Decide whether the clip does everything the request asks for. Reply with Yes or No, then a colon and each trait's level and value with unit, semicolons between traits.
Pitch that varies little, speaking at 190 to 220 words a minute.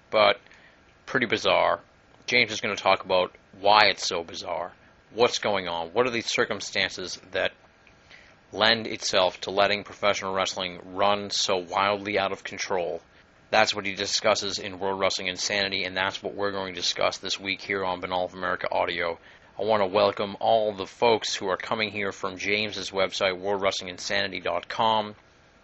No: narrow, 2.1 semitones; average, 165 wpm